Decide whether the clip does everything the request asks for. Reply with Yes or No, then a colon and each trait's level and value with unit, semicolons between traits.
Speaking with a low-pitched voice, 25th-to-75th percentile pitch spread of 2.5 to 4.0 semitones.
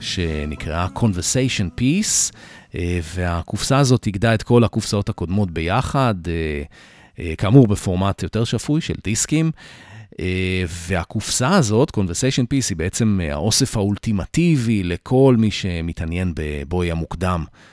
No: low, 100 Hz; average, 4.8 semitones